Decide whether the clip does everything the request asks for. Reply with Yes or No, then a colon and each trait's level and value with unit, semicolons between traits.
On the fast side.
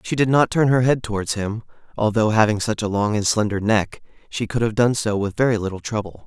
Yes: fast, 240 wpm